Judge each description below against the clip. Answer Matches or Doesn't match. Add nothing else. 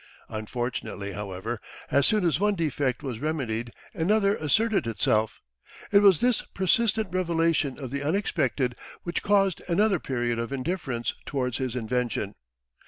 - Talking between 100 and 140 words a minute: Matches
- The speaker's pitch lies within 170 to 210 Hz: Doesn't match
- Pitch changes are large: Matches